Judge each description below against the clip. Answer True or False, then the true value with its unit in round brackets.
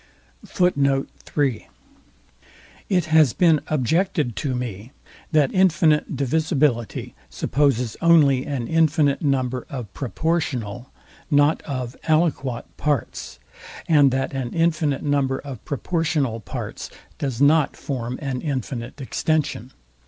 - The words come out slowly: True (100 wpm)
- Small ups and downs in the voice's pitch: False (3.8 semitones)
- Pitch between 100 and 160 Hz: True (140 Hz)